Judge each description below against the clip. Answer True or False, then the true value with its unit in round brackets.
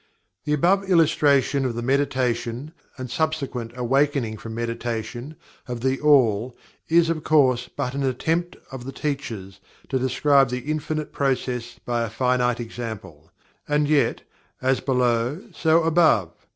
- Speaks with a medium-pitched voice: False (130 Hz)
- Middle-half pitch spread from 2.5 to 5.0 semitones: True (3.8 semitones)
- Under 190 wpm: True (140 wpm)